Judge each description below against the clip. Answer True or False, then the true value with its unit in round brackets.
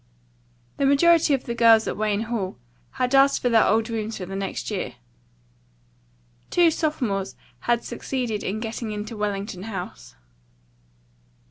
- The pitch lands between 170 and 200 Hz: False (225 Hz)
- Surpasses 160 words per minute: False (140 wpm)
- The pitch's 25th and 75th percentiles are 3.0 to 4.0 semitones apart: True (3.6 semitones)